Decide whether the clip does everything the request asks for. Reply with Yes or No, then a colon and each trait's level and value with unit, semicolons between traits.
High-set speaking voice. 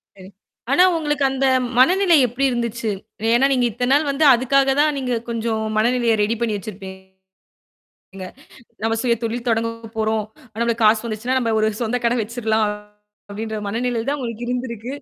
Yes: high, 235 Hz